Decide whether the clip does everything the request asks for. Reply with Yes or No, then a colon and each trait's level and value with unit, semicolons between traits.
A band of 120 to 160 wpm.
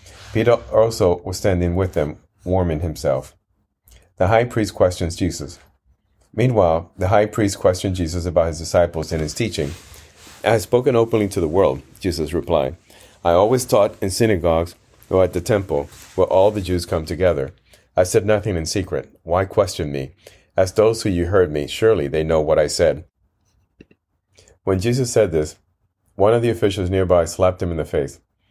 No: average, 175 wpm